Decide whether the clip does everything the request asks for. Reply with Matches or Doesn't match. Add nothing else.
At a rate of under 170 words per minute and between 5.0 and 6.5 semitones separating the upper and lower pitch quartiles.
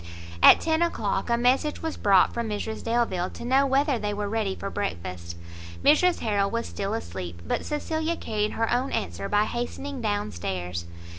Doesn't match